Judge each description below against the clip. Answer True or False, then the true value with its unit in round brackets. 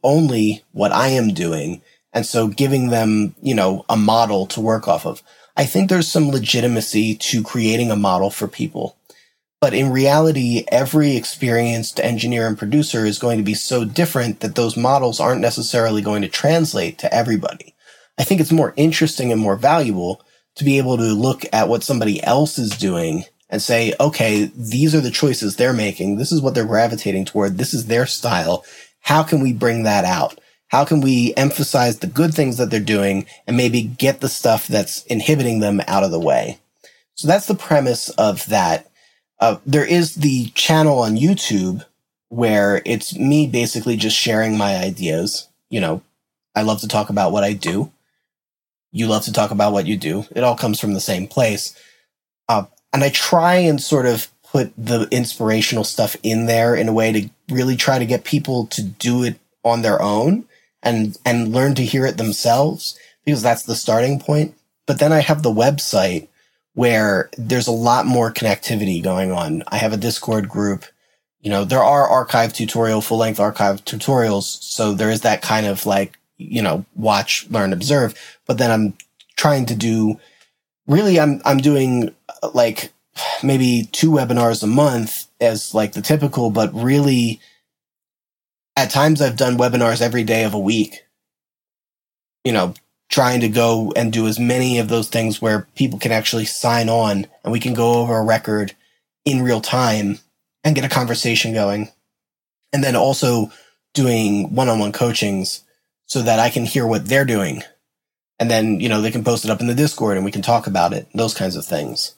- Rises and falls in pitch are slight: False (3.8 semitones)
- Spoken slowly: False (185 wpm)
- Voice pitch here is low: True (115 Hz)